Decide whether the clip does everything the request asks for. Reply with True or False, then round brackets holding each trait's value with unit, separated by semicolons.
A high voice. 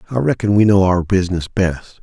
False (100 Hz)